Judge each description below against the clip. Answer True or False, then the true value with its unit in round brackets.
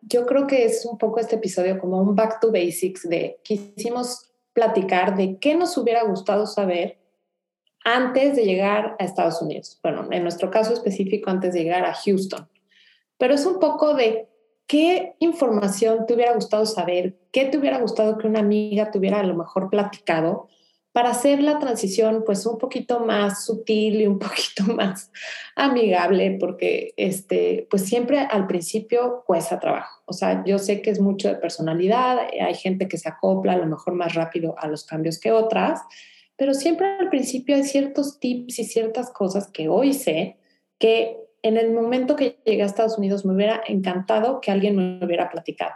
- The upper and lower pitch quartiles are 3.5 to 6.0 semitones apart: True (4.2 semitones)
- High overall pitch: True (220 Hz)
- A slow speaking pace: False (180 wpm)